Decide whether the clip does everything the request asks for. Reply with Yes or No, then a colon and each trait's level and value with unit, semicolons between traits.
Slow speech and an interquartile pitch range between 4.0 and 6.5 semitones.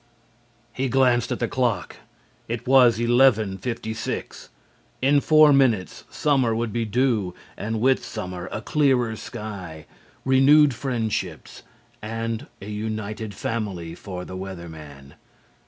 Yes: slow, 120 wpm; average, 4.7 semitones